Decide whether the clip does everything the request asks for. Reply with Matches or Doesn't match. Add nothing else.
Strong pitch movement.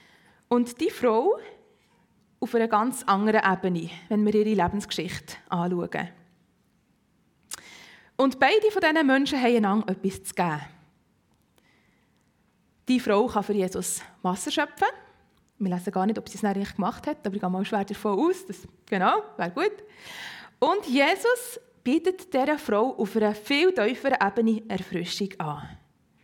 Matches